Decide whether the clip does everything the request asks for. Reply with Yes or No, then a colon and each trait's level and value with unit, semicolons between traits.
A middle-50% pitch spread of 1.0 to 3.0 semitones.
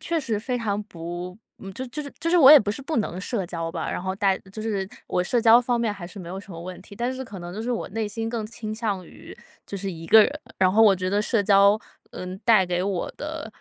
No: average, 4.1 semitones